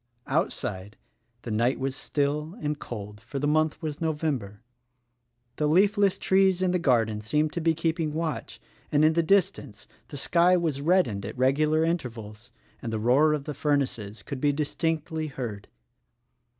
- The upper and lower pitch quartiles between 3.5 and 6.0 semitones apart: Yes, average, 5.2 semitones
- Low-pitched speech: No, medium, 150 Hz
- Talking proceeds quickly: No, average, 165 wpm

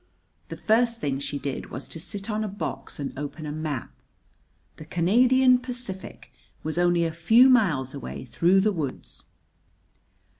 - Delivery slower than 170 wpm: Yes, average, 155 wpm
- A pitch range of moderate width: No, wide, 7.1 semitones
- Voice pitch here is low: No, medium, 175 Hz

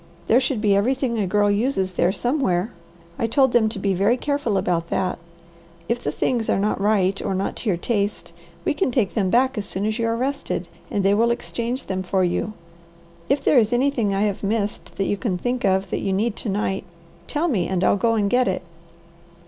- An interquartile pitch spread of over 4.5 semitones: No, average, 3.9 semitones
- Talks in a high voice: Yes, high, 210 Hz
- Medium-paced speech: No, fast, 220 wpm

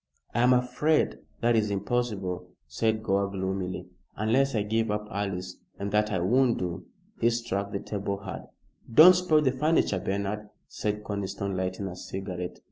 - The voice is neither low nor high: No, low, 105 Hz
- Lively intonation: No, average, 3.6 semitones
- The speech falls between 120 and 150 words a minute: No, average, 160 wpm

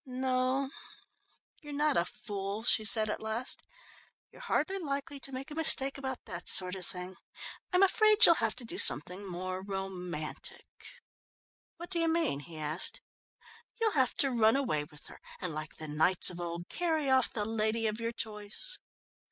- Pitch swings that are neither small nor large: No, wide, 7.2 semitones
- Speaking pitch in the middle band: No, high, 225 Hz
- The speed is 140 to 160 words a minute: No, average, 175 wpm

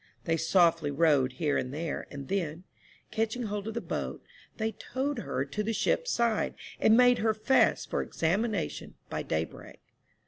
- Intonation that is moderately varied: No, wide, 6.5 semitones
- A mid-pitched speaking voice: No, high, 195 Hz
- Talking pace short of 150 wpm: No, average, 165 wpm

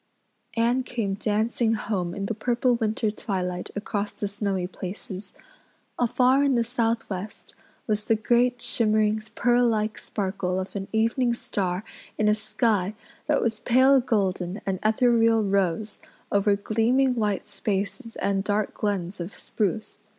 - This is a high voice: Yes, high, 215 Hz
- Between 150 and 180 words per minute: No, average, 140 wpm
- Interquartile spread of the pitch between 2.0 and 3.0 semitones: Yes, average, 2.7 semitones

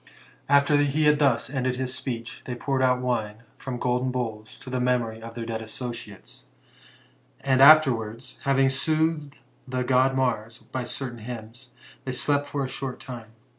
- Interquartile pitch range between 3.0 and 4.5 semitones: No, narrow, 2.5 semitones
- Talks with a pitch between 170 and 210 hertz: No, low, 125 Hz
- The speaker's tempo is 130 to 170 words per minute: Yes, average, 165 wpm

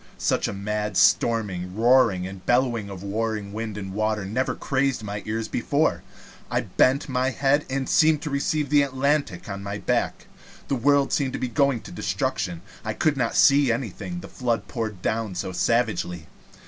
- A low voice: Yes, low, 115 Hz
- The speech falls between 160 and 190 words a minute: Yes, average, 165 wpm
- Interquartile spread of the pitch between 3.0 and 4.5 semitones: No, average, 5.2 semitones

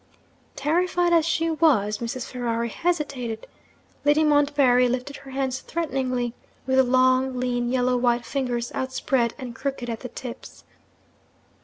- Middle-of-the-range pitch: No, very high, 255 Hz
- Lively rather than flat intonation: No, average, 2.8 semitones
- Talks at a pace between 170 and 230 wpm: No, slow, 135 wpm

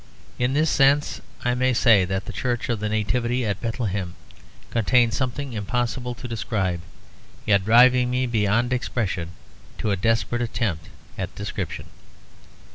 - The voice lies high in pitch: No, low, 120 Hz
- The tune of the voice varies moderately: Yes, average, 3.2 semitones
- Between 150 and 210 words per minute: No, average, 140 wpm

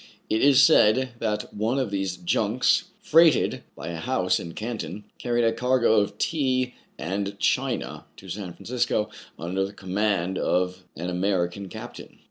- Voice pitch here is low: Yes, low, 105 Hz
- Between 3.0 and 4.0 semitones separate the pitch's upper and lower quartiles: No, average, 4.7 semitones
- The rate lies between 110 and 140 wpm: No, average, 150 wpm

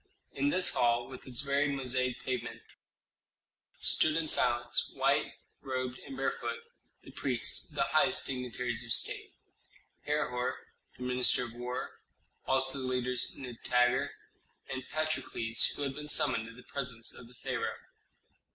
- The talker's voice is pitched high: No, low, 125 Hz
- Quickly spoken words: No, average, 140 wpm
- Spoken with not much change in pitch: Yes, narrow, 1.8 semitones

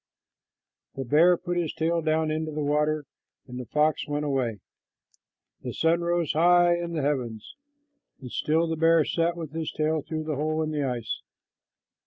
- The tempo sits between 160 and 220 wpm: Yes, average, 175 wpm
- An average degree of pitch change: No, narrow, 2.1 semitones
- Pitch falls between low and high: Yes, medium, 155 Hz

